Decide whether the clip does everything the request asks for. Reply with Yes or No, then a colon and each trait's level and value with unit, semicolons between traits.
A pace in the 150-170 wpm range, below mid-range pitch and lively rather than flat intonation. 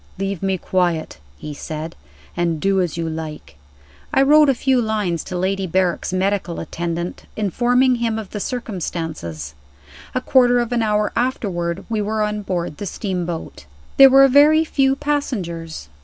No: average, 155 wpm; high, 195 Hz; wide, 6.1 semitones